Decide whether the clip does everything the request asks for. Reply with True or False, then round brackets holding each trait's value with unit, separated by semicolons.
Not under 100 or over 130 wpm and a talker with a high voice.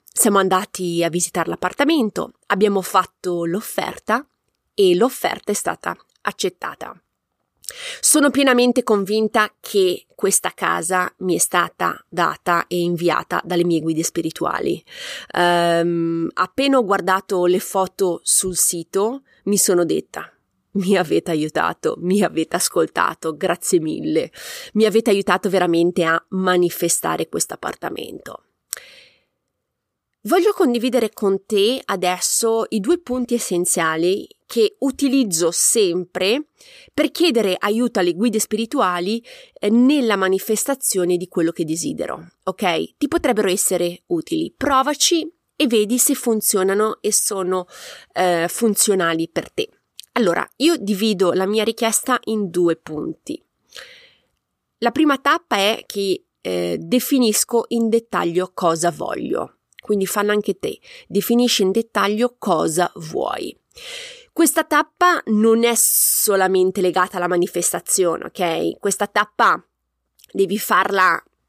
True (115 wpm; 205 Hz)